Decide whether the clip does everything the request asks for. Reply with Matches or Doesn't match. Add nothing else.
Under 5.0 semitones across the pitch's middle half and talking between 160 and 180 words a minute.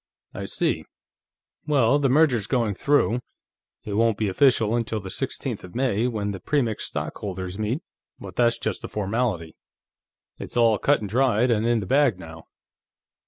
Matches